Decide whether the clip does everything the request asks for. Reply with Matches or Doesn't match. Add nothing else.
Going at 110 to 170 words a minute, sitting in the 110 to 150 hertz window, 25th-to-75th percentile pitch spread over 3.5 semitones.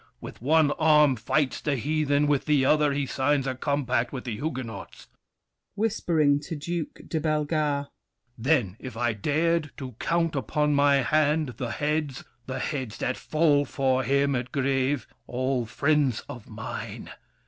Doesn't match